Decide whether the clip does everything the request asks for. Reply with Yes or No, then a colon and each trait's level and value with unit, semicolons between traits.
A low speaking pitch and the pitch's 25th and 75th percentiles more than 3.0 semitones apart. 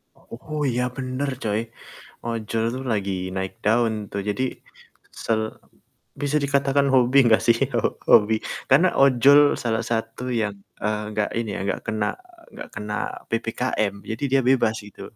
Yes: low, 115 Hz; average, 3.6 semitones